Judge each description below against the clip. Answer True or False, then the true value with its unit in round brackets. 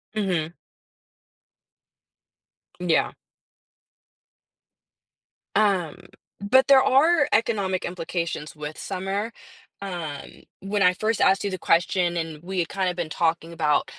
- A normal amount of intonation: True (3.4 semitones)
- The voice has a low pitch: False (185 Hz)